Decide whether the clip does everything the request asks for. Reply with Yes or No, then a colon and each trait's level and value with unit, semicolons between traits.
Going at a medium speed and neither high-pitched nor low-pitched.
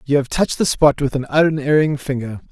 No: fast, 215 wpm; medium, 145 Hz